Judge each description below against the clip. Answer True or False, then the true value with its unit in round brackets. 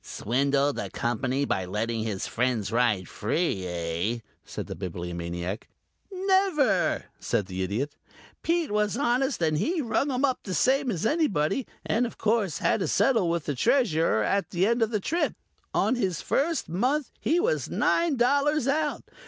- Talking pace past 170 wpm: False (160 wpm)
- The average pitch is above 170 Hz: True (185 Hz)